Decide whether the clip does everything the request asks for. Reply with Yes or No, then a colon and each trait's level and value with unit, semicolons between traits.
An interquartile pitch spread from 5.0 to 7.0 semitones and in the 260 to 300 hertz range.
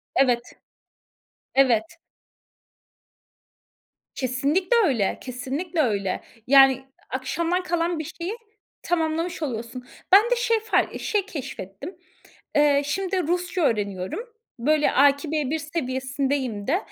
Yes: average, 5.3 semitones; very high, 285 Hz